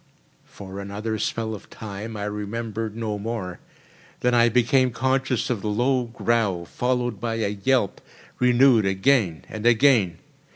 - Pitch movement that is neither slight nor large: Yes, average, 3.1 semitones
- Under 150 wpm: Yes, average, 140 wpm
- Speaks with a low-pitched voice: Yes, low, 115 Hz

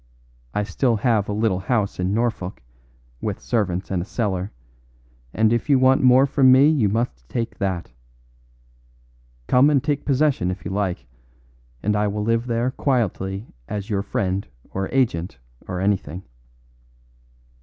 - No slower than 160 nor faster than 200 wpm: No, average, 150 wpm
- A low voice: Yes, low, 105 Hz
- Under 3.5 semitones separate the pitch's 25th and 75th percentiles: No, average, 4.7 semitones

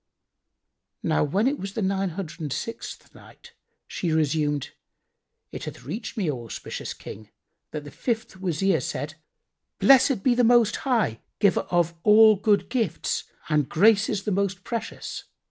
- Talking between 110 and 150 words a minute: Yes, average, 145 wpm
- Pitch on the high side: Yes, high, 195 Hz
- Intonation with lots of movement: Yes, wide, 6.1 semitones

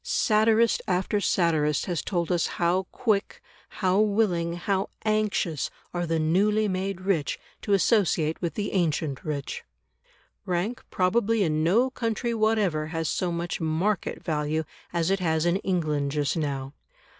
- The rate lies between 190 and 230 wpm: No, average, 145 wpm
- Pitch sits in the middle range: Yes, medium, 180 Hz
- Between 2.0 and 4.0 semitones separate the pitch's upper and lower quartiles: No, average, 4.4 semitones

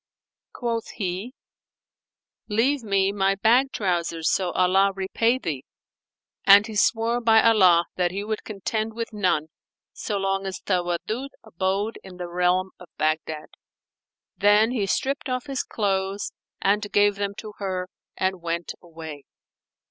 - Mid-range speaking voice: No, high, 195 Hz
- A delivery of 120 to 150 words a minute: Yes, average, 140 wpm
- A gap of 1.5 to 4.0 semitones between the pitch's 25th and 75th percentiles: Yes, average, 3.4 semitones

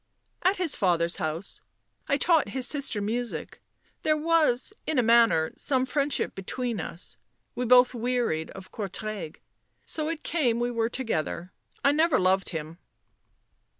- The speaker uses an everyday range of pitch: No, wide, 6.7 semitones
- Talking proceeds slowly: No, average, 150 wpm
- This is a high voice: Yes, high, 240 Hz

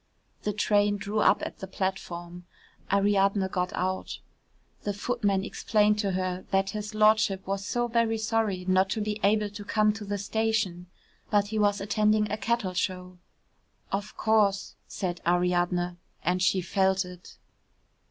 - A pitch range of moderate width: No, narrow, 2.2 semitones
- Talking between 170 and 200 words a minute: No, average, 150 wpm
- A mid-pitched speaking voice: No, high, 200 Hz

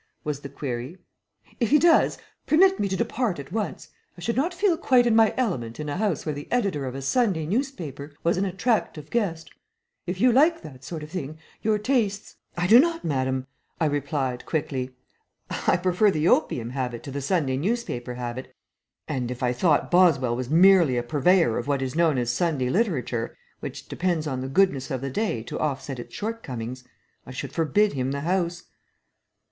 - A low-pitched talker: No, medium, 155 Hz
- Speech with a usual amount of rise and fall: No, wide, 7.7 semitones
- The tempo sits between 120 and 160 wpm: No, average, 195 wpm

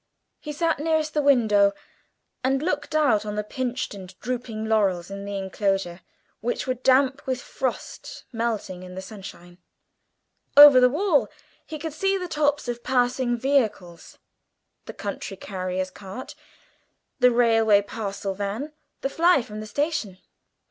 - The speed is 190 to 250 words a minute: No, average, 145 wpm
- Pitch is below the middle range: No, high, 235 Hz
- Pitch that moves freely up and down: Yes, wide, 5.9 semitones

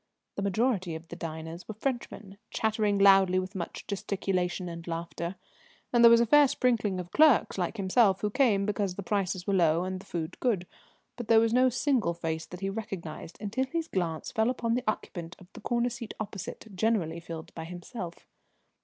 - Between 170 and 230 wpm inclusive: Yes, average, 190 wpm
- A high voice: Yes, high, 195 Hz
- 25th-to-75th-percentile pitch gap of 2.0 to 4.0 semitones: No, average, 4.5 semitones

